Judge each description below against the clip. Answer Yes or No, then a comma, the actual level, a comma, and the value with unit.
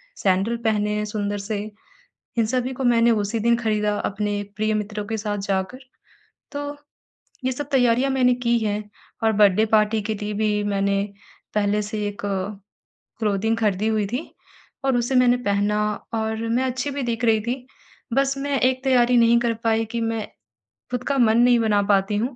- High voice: Yes, high, 220 Hz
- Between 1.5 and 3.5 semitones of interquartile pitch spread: Yes, average, 2.8 semitones